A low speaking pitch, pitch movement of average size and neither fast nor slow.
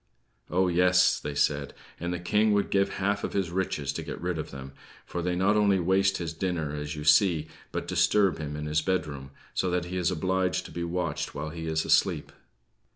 No: very low, 90 Hz; average, 3.4 semitones; fast, 215 wpm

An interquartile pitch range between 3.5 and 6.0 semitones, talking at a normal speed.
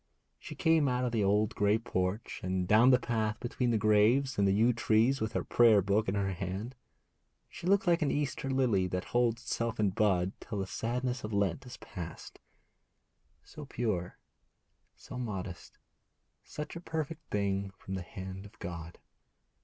Yes: average, 4.4 semitones; average, 175 wpm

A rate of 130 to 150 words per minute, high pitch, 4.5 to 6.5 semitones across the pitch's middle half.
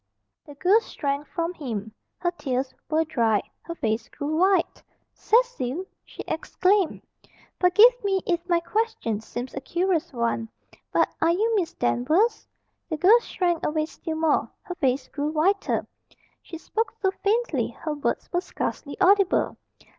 Yes: average, 145 wpm; very high, 335 Hz; average, 5.3 semitones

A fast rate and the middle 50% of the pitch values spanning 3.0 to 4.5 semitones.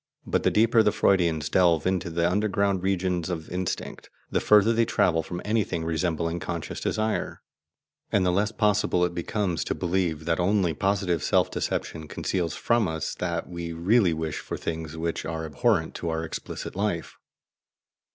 No: average, 165 wpm; average, 3.4 semitones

